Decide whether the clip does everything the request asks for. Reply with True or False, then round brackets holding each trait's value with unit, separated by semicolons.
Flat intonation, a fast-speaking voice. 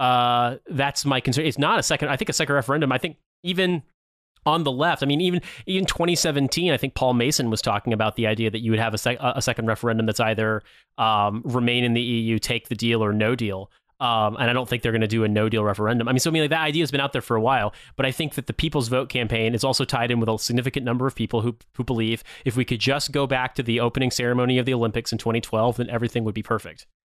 False (3.4 semitones; 275 wpm)